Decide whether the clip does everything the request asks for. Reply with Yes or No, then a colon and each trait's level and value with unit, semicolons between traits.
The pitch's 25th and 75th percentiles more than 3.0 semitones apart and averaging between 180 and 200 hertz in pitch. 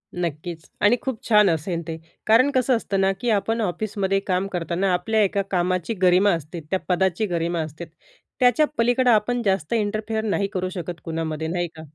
Yes: average, 4.0 semitones; high, 190 Hz